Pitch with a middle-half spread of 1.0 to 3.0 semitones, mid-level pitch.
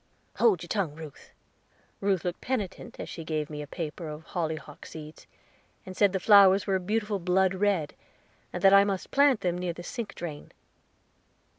No: average, 3.9 semitones; medium, 180 Hz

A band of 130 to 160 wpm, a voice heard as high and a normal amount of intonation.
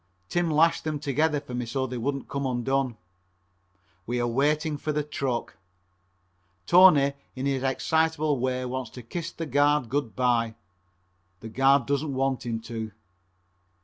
No: average, 150 wpm; low, 135 Hz; average, 3.2 semitones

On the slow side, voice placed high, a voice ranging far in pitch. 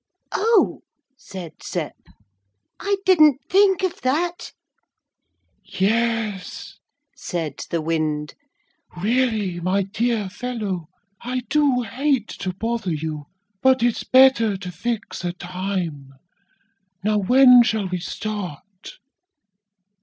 Yes: slow, 100 wpm; high, 215 Hz; wide, 5.9 semitones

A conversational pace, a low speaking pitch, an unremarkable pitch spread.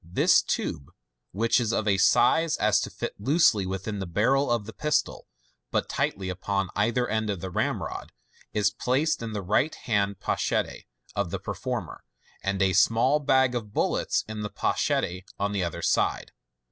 Yes: average, 175 wpm; low, 105 Hz; average, 3.8 semitones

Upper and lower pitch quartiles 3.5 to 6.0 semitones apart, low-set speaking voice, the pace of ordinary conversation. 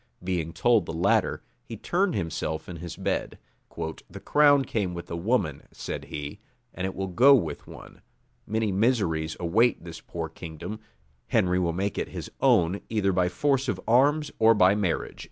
Yes: wide, 5.5 semitones; very low, 95 Hz; average, 170 wpm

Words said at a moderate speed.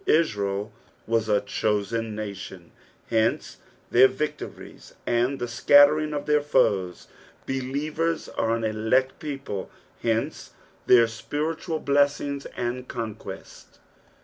No: slow, 105 wpm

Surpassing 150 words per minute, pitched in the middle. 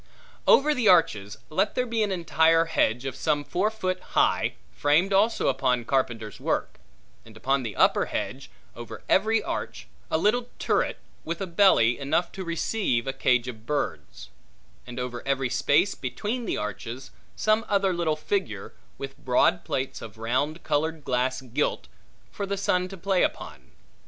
Yes: average, 160 wpm; medium, 155 Hz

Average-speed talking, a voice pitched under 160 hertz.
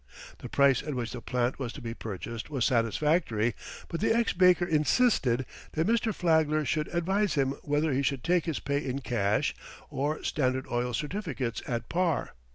Yes: average, 175 wpm; medium, 140 Hz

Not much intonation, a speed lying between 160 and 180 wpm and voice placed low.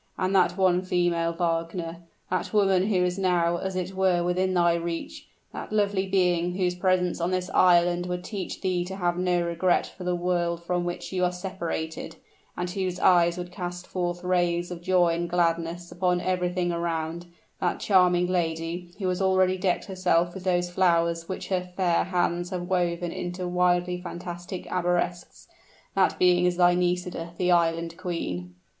No: narrow, 1.0 semitones; average, 170 wpm; medium, 180 Hz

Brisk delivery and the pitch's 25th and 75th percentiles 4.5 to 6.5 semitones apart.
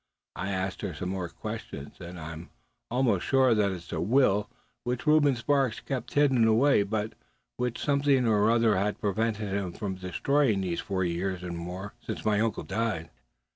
No: average, 175 wpm; average, 4.8 semitones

